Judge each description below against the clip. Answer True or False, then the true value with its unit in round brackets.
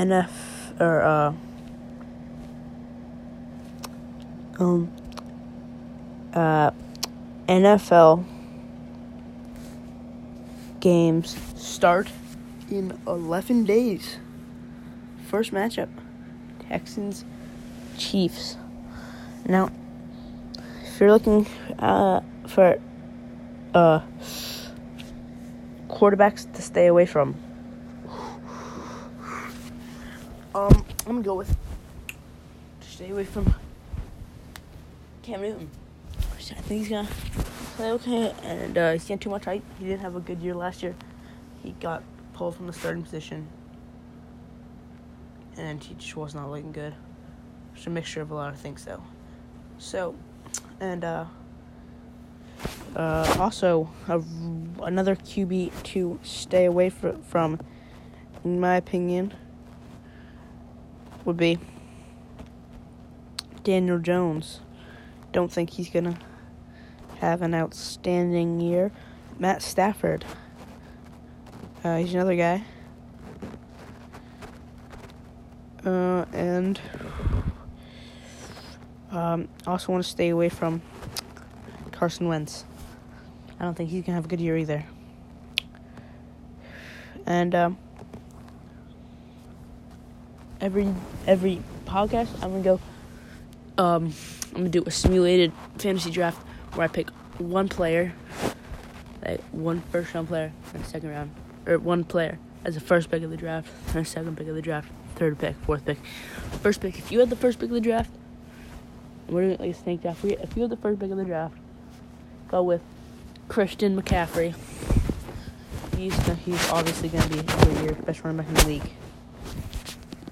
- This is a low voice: False (150 Hz)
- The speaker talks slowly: True (115 wpm)